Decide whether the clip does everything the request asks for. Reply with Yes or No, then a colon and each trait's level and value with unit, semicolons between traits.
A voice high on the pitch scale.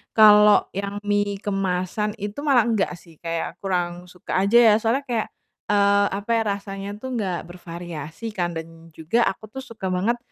Yes: high, 200 Hz